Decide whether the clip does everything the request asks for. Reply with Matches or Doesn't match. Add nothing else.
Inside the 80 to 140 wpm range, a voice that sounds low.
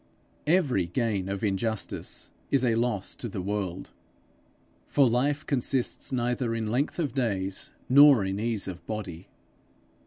Matches